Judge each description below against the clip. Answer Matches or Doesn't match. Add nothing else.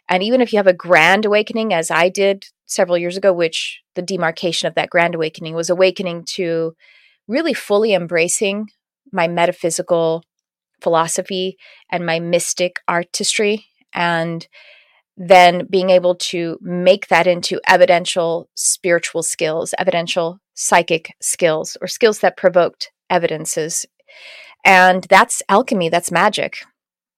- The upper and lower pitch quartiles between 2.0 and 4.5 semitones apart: Matches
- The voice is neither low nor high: Matches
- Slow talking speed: Matches